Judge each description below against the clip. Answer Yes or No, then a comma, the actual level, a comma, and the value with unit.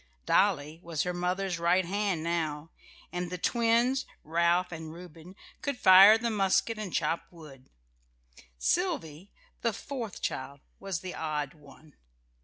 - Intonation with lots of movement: No, average, 4.1 semitones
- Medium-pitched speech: Yes, medium, 180 Hz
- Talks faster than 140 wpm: No, slow, 135 wpm